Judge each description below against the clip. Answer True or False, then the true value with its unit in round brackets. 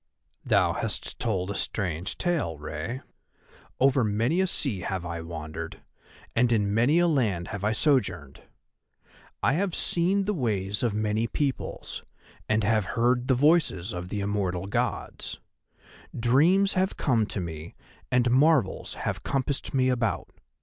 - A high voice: False (115 Hz)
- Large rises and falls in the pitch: True (6.3 semitones)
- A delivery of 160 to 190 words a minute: False (145 wpm)